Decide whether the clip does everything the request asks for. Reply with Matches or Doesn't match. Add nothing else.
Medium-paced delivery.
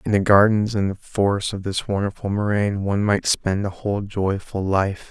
Matches